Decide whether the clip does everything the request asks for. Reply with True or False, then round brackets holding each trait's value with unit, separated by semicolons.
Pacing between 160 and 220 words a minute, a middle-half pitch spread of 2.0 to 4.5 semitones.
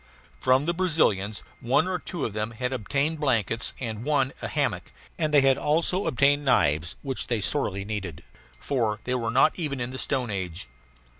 False (180 wpm; 5.3 semitones)